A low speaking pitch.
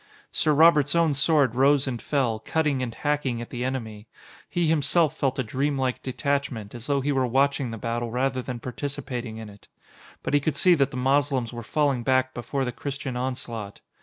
Yes: low, 130 Hz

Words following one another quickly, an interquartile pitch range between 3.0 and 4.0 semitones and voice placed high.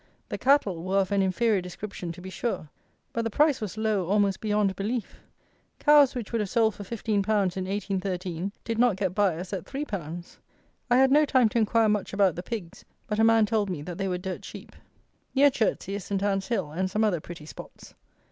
Yes: fast, 210 wpm; average, 3.3 semitones; high, 200 Hz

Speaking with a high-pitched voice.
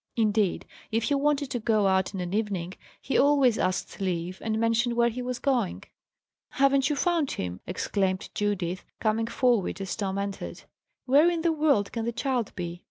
Yes: high, 225 Hz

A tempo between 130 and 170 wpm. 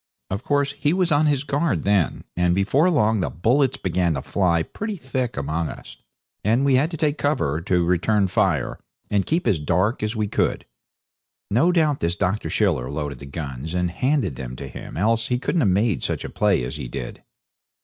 No: average, 200 wpm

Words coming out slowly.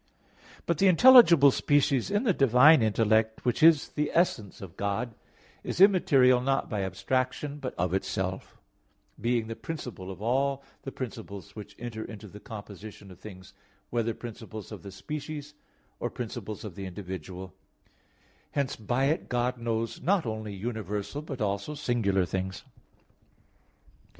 No: average, 145 wpm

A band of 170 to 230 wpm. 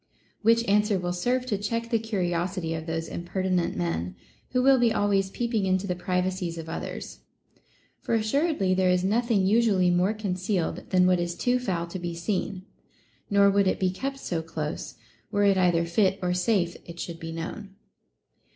Yes: average, 180 wpm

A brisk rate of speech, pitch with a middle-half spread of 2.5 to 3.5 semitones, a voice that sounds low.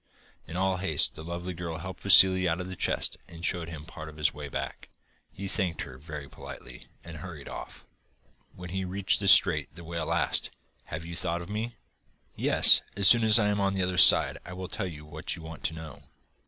Yes: fast, 220 wpm; average, 2.8 semitones; very low, 85 Hz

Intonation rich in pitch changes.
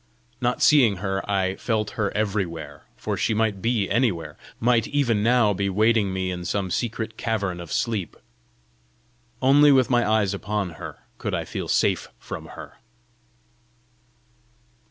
No: average, 3.5 semitones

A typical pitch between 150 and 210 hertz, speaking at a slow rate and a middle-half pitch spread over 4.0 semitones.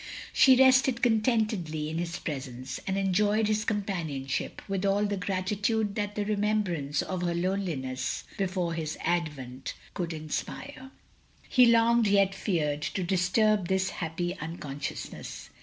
Yes: high, 190 Hz; slow, 130 wpm; average, 4.6 semitones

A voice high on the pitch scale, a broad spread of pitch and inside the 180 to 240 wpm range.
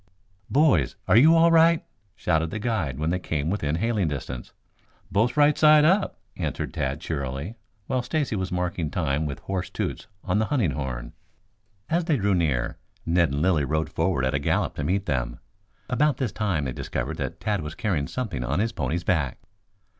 No: very low, 90 Hz; wide, 8.5 semitones; average, 185 wpm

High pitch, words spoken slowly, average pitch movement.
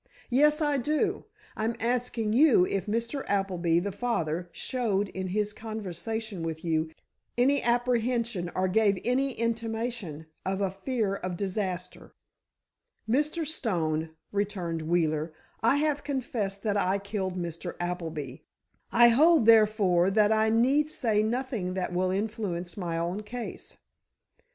Yes: high, 210 Hz; slow, 130 wpm; average, 4.8 semitones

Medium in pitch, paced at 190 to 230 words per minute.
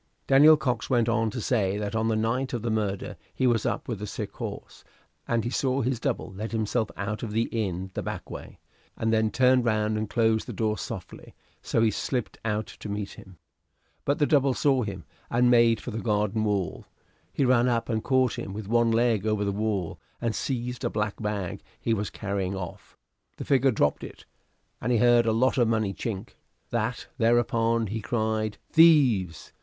No: low, 115 Hz; average, 200 wpm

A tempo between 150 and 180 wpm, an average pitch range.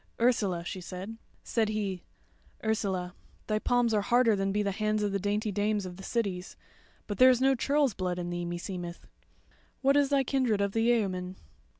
No: average, 190 wpm; average, 3.9 semitones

